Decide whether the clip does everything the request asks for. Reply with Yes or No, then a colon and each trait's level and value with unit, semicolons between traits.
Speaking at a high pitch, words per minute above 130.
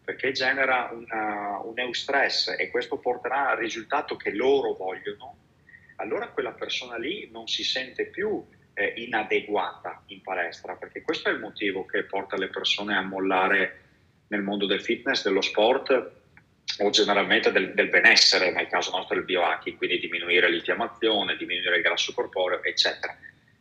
Yes: very high, 370 Hz; average, 155 wpm